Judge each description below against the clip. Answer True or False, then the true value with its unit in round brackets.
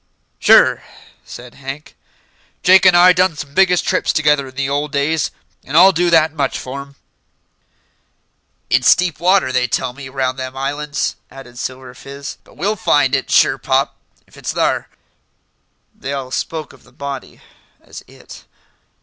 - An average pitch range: True (3.4 semitones)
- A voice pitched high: False (140 Hz)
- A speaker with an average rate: True (160 wpm)